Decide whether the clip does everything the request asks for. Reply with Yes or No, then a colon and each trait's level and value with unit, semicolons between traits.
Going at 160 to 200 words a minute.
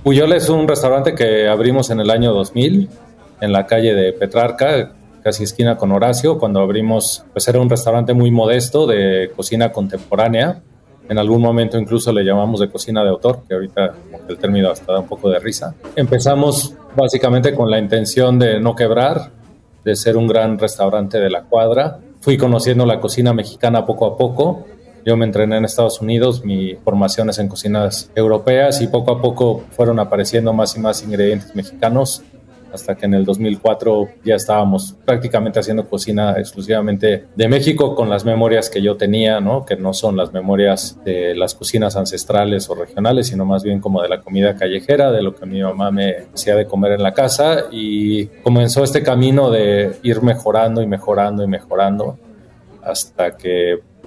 Yes: average, 180 wpm